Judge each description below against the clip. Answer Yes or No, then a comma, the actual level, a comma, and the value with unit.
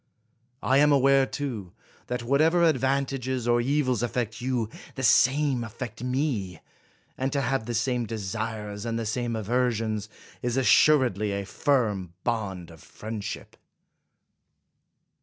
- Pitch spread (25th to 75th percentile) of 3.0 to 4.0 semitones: Yes, average, 3.5 semitones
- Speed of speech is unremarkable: No, slow, 130 wpm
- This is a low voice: Yes, low, 120 Hz